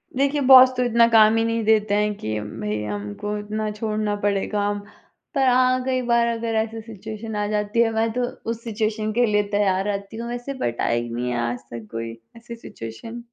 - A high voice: Yes, high, 215 Hz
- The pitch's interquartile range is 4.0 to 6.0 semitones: No, narrow, 2.4 semitones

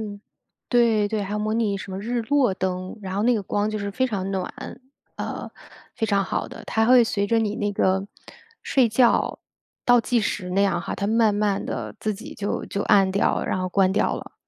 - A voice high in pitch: Yes, high, 205 Hz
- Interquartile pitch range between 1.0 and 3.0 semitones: Yes, narrow, 2.5 semitones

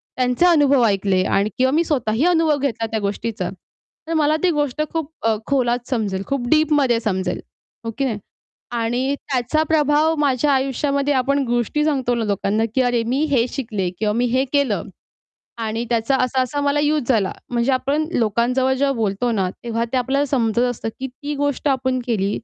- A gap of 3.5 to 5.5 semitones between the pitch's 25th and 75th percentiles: Yes, average, 3.9 semitones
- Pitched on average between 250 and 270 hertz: Yes, very high, 255 Hz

